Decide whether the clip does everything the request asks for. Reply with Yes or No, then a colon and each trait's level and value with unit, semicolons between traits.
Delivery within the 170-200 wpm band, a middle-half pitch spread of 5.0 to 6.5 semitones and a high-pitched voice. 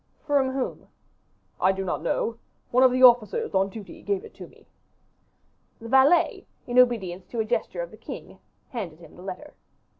Yes: average, 180 wpm; wide, 5.4 semitones; high, 235 Hz